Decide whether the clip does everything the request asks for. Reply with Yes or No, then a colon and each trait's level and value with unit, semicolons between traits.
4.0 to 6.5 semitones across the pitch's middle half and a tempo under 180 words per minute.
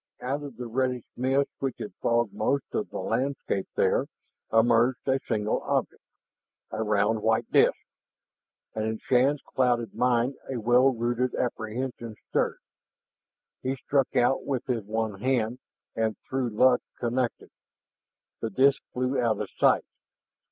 No: average, 2.7 semitones; average, 140 wpm